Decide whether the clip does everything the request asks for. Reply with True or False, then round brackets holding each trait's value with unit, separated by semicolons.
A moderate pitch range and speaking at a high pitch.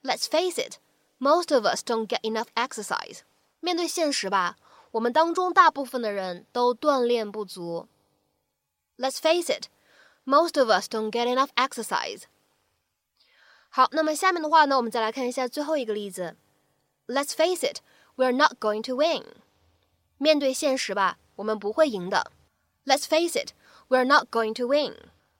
False (5.8 semitones; 260 Hz)